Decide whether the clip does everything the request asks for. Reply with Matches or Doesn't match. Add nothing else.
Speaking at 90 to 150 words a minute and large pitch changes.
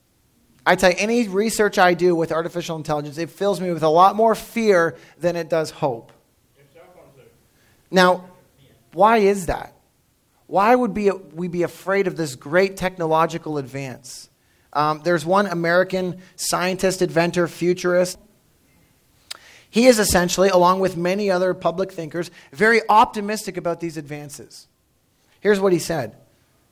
Doesn't match